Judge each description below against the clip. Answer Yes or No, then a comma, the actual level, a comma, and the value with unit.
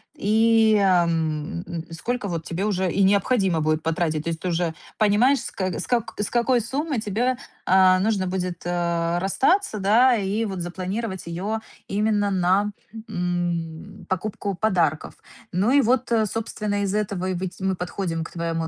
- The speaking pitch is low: No, high, 190 Hz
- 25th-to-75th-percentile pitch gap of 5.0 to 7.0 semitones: No, average, 3.8 semitones